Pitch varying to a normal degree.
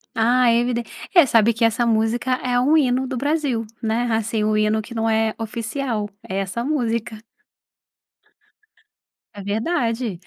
No: narrow, 2.2 semitones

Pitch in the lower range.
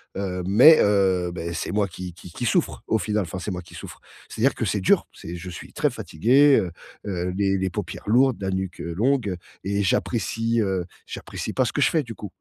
Yes: very low, 95 Hz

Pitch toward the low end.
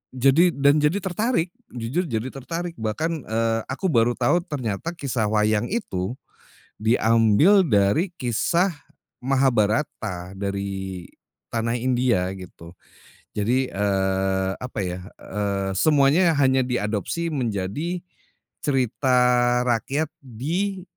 Yes: low, 120 Hz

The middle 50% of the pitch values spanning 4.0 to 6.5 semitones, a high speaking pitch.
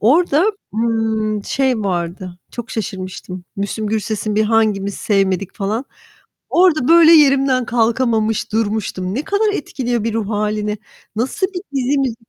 Yes: average, 4.3 semitones; high, 225 Hz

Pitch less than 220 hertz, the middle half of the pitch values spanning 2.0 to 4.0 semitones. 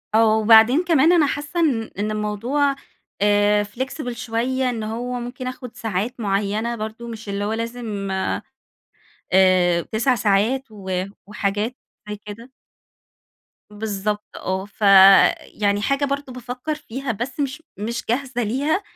No: high, 225 Hz; average, 3.7 semitones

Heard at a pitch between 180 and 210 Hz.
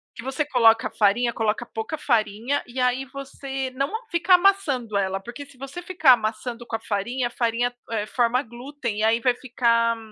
No: high, 245 Hz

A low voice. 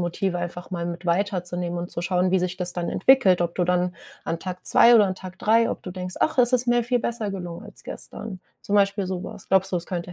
No: medium, 185 Hz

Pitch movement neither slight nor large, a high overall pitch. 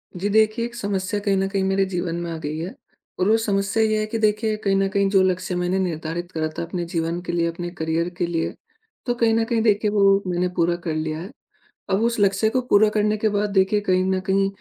Yes: average, 3.4 semitones; high, 195 Hz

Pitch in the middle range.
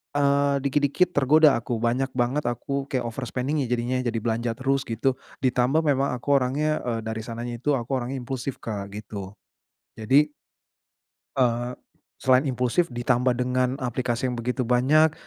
No: low, 125 Hz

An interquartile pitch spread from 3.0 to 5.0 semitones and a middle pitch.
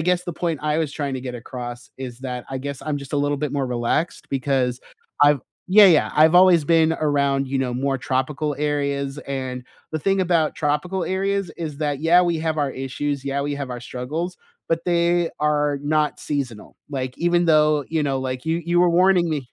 Yes: average, 3.5 semitones; medium, 145 Hz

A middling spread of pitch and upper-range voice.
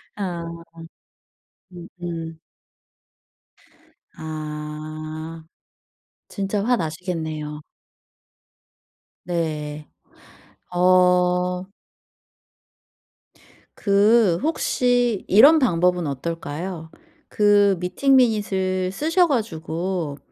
No: average, 4.2 semitones; medium, 180 Hz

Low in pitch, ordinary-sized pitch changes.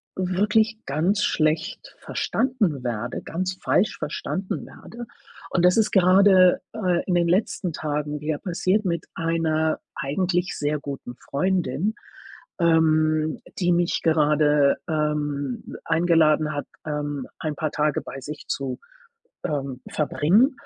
No: medium, 160 Hz; average, 3.7 semitones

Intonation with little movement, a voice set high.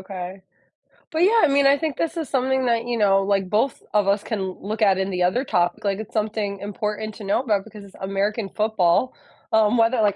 No: average, 3.6 semitones; high, 210 Hz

